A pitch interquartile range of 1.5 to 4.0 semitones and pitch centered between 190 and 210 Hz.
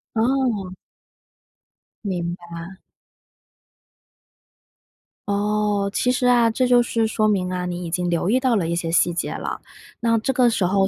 No: average, 4.8 semitones; high, 205 Hz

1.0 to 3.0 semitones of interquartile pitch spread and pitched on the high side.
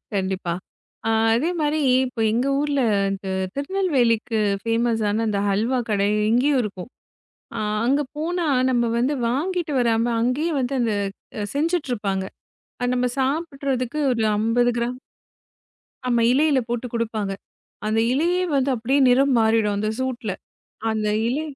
No: average, 4.0 semitones; high, 245 Hz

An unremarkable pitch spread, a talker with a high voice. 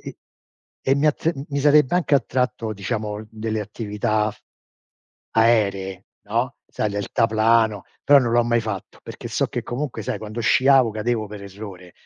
No: average, 3.1 semitones; low, 110 Hz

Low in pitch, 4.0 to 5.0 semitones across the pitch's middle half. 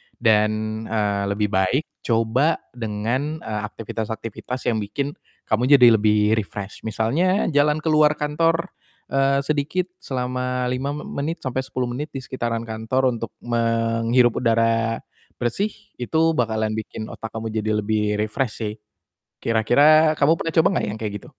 Yes: low, 120 Hz; average, 4.5 semitones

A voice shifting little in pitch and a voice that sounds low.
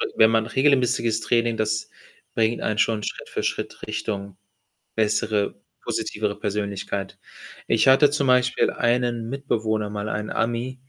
Yes: narrow, 2.3 semitones; low, 110 Hz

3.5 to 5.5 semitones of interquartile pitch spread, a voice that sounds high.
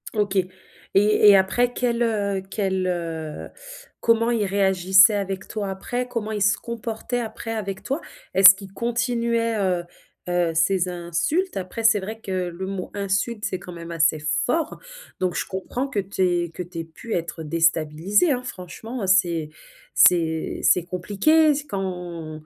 Yes: average, 4.3 semitones; high, 195 Hz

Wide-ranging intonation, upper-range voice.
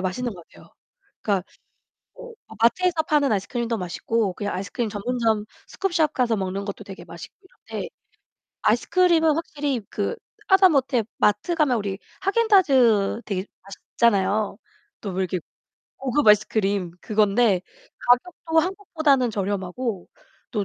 Yes: wide, 7.1 semitones; high, 230 Hz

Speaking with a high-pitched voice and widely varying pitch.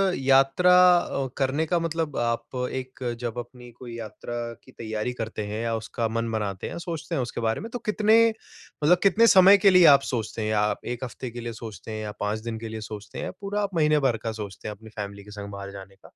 No: low, 120 Hz; wide, 5.9 semitones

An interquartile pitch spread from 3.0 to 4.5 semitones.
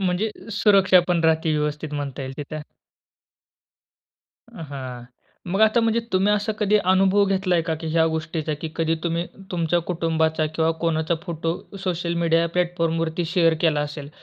No: narrow, 2.4 semitones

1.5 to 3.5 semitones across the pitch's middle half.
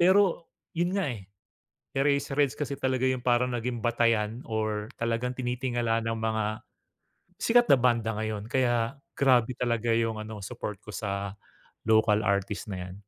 Yes: average, 3.1 semitones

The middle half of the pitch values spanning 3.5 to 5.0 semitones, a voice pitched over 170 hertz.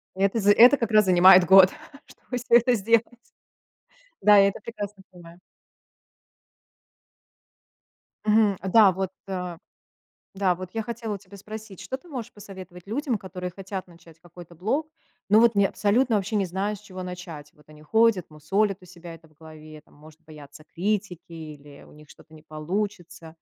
Yes: average, 3.9 semitones; high, 190 Hz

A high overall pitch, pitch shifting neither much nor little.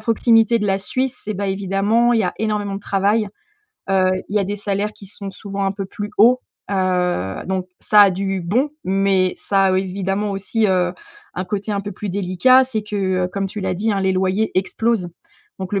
No: high, 195 Hz; narrow, 1.9 semitones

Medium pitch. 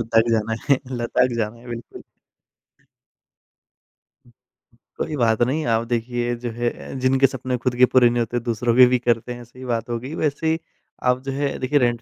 No: low, 120 Hz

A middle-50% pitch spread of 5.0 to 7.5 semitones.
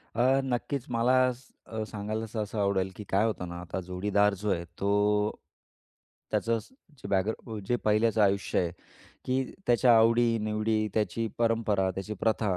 No: narrow, 2.4 semitones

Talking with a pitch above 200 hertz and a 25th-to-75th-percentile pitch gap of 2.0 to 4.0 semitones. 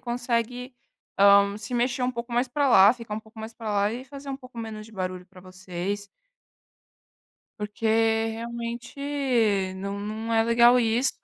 Yes: high, 230 Hz; average, 3.3 semitones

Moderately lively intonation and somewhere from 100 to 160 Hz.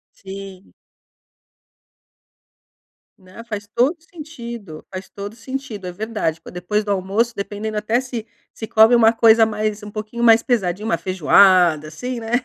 No: average, 3.3 semitones; high, 215 Hz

